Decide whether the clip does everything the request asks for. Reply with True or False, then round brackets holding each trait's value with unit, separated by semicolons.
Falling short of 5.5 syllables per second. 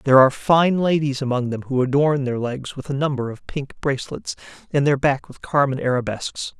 False (5.6 syllables/s)